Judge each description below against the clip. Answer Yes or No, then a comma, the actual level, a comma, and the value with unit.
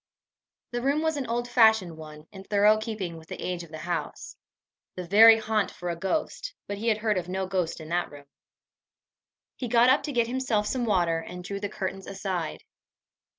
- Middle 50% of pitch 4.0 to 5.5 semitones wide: Yes, average, 4.7 semitones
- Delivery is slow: No, average, 200 wpm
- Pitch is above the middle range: Yes, high, 200 Hz